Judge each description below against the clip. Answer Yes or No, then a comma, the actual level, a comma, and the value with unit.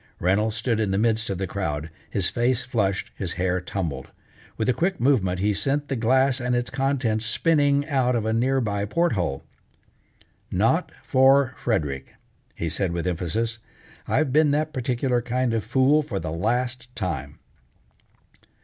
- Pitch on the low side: Yes, low, 115 Hz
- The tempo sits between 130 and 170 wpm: Yes, average, 165 wpm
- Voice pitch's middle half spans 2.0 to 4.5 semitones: No, wide, 5.4 semitones